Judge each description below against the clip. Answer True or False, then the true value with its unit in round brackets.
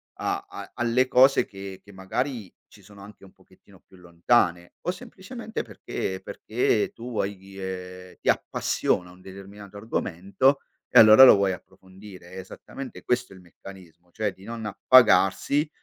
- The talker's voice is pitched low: True (100 Hz)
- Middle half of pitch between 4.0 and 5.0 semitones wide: True (4.3 semitones)